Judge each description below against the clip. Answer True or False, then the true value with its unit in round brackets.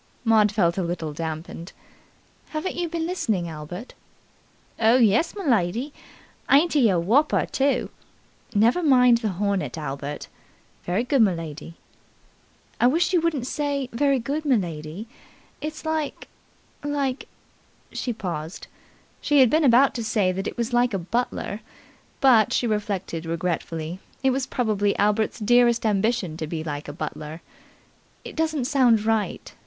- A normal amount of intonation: False (7.3 semitones)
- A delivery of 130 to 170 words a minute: True (145 wpm)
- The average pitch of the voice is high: True (225 Hz)